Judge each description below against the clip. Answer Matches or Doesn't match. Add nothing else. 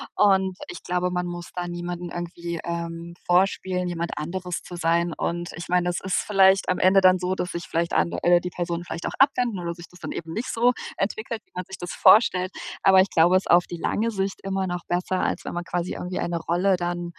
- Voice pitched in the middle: Matches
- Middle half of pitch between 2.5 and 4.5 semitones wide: Doesn't match